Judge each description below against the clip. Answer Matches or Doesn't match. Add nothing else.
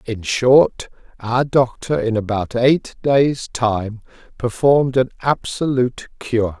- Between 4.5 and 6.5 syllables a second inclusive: Doesn't match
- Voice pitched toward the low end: Matches